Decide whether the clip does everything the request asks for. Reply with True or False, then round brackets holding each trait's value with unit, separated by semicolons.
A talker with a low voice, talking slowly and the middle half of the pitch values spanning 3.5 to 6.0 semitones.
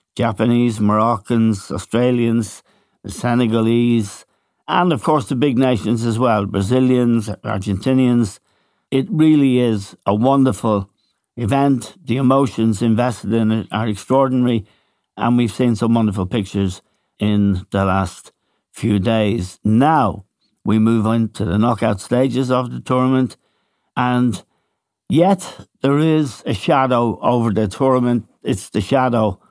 False (115 Hz; 125 wpm; 3.1 semitones)